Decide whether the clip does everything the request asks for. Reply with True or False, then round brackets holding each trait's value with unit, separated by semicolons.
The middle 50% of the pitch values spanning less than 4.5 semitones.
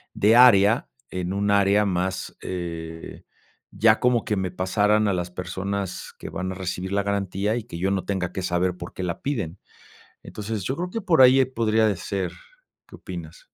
True (3.1 semitones)